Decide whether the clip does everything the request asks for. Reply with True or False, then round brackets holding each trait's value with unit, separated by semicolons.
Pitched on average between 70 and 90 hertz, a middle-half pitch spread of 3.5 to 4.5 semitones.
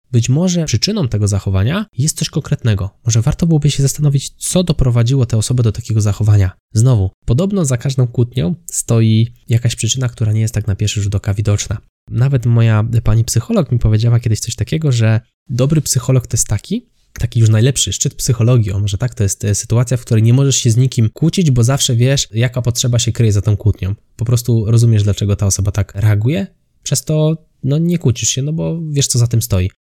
False (120 Hz; 4.0 semitones)